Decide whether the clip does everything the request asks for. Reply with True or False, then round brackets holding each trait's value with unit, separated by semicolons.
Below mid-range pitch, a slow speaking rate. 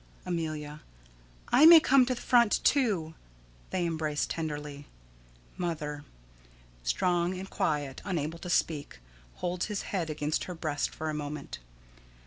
False (165 Hz; 130 wpm)